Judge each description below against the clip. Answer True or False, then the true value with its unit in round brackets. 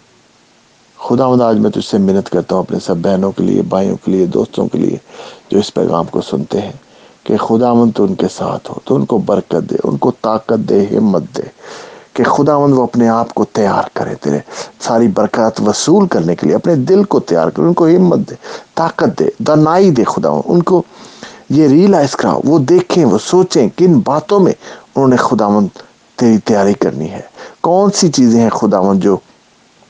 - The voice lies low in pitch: True (125 Hz)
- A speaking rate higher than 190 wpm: True (200 wpm)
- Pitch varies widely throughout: True (8.9 semitones)